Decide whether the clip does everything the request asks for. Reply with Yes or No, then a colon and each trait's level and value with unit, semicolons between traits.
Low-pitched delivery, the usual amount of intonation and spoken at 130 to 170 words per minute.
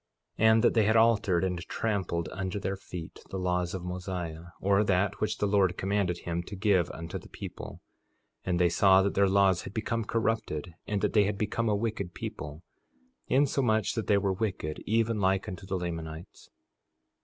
No: very low, 95 Hz; average, 3.1 semitones; average, 190 wpm